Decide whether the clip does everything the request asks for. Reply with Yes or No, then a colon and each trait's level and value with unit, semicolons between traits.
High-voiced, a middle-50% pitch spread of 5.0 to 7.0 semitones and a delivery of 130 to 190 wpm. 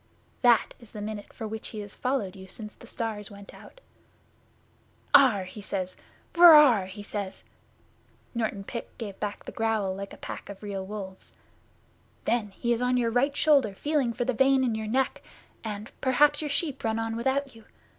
No: high, 225 Hz; average, 4.0 semitones; average, 185 wpm